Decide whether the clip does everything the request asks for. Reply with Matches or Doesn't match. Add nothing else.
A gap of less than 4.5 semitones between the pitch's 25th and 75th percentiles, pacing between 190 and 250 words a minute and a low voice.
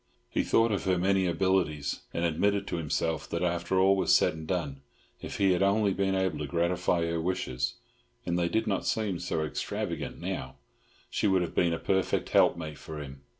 Matches